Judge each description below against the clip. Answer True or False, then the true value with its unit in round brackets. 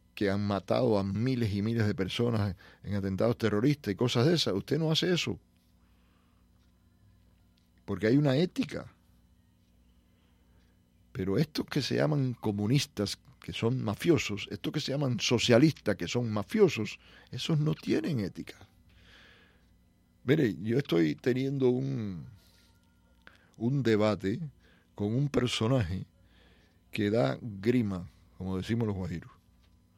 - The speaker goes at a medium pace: False (125 wpm)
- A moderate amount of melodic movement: False (5.9 semitones)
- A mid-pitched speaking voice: False (105 Hz)